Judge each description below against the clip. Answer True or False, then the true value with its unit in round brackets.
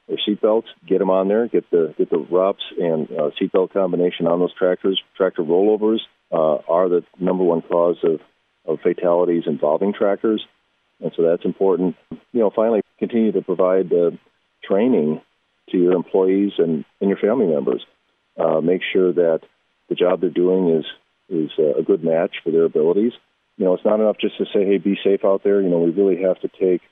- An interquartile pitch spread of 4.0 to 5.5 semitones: False (3.4 semitones)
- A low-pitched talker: True (95 Hz)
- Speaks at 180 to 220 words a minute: True (200 wpm)